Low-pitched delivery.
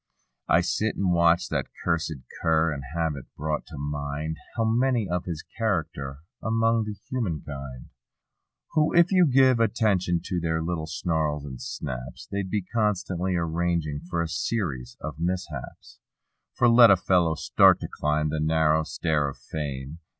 Yes: very low, 85 Hz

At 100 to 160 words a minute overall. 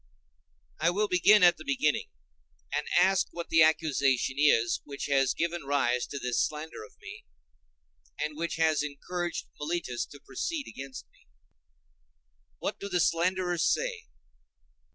Yes: average, 140 wpm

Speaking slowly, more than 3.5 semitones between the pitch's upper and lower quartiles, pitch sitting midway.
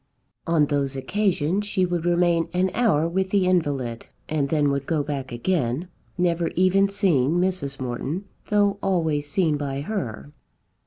No: average, 150 wpm; average, 4.8 semitones; medium, 165 Hz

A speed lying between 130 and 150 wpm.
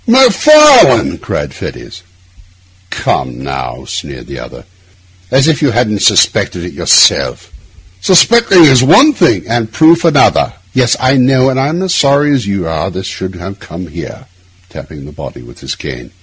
No: average, 160 wpm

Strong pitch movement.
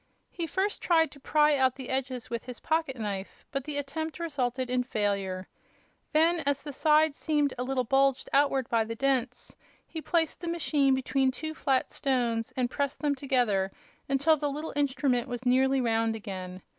No: average, 3.3 semitones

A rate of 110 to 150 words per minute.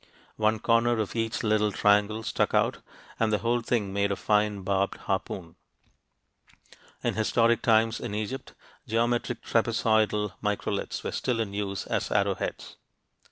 Yes: average, 140 wpm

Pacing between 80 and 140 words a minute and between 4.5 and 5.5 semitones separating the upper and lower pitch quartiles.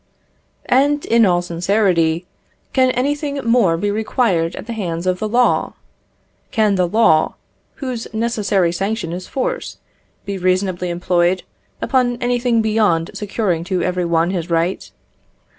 Yes: slow, 135 wpm; average, 5.0 semitones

